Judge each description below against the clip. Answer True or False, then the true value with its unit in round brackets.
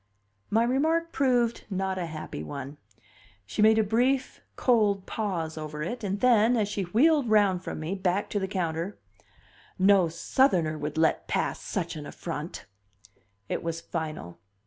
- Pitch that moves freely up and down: True (5.7 semitones)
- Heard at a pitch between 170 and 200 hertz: True (190 Hz)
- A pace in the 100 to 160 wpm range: True (155 wpm)